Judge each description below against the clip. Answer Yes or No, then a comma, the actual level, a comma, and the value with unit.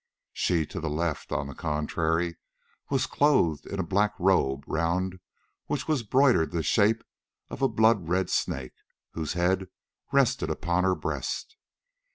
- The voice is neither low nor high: No, very low, 90 Hz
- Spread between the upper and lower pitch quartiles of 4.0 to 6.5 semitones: Yes, average, 4.6 semitones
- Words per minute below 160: Yes, average, 150 wpm